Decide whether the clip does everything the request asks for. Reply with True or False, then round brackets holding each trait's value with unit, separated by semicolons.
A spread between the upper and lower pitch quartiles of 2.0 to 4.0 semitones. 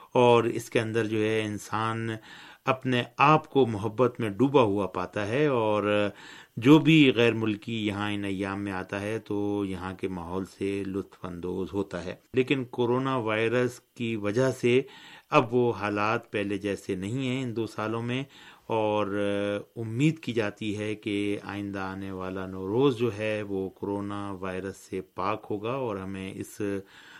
True (3.4 semitones)